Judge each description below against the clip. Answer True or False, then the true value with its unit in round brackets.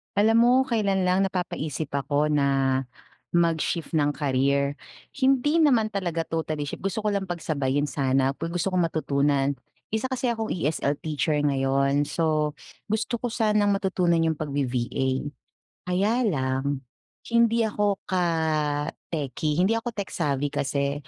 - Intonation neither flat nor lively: False (6.5 semitones)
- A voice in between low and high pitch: True (165 Hz)